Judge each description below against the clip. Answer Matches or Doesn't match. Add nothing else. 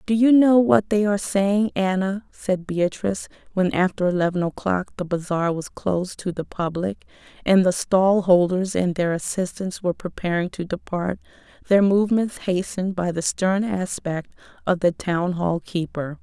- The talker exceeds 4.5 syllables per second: Matches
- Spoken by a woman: Matches